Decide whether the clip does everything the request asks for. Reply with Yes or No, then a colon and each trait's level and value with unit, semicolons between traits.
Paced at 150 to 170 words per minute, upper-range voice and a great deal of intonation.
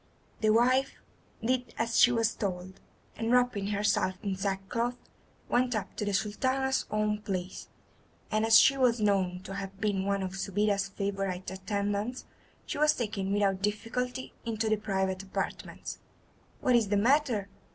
No: average, 155 wpm; high, 210 Hz; average, 3.3 semitones